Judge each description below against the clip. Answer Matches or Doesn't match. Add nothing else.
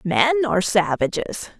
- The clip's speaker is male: Doesn't match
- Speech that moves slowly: Matches